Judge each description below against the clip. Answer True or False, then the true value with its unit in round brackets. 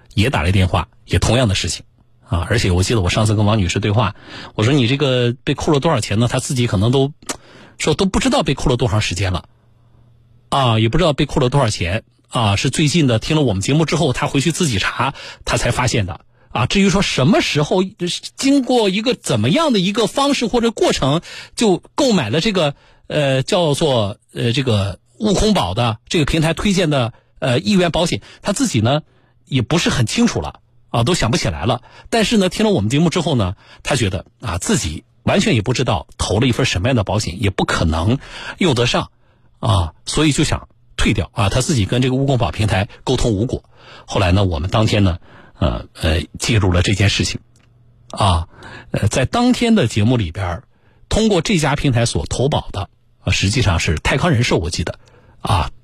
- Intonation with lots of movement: True (6.2 semitones)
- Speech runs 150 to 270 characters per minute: False (295 characters per minute)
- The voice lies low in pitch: True (120 Hz)